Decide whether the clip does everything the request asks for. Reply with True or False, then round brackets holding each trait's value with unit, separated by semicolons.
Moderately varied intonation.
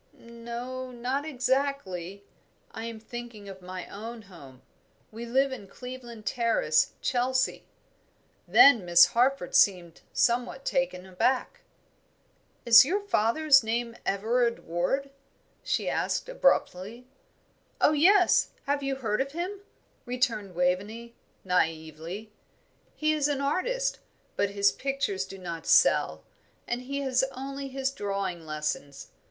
False (5.8 semitones)